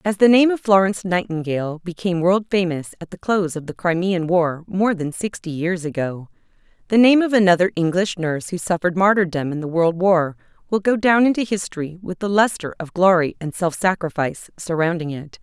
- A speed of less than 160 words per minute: No, average, 190 wpm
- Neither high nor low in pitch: Yes, medium, 180 Hz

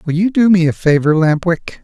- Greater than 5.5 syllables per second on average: No, 5.3 syllables/s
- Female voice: No, male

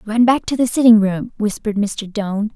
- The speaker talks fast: Yes, fast, 210 wpm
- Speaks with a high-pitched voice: Yes, high, 215 Hz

